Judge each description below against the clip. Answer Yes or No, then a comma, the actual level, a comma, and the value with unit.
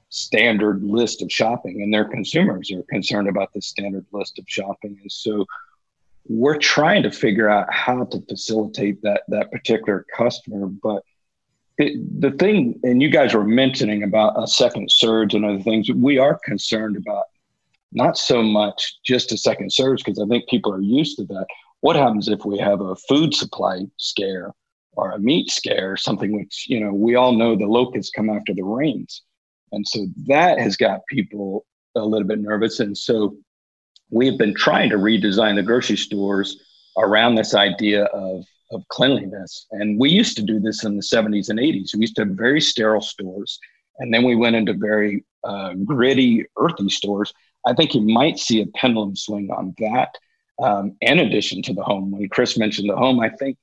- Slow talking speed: No, average, 185 wpm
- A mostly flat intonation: Yes, narrow, 1.9 semitones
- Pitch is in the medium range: No, low, 105 Hz